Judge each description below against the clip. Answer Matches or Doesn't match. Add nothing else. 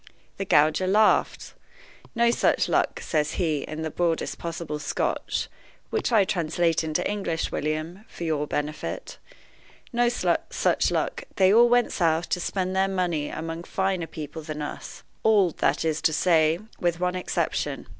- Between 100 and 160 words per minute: Matches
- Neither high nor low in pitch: Matches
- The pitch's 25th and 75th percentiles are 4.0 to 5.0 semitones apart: Doesn't match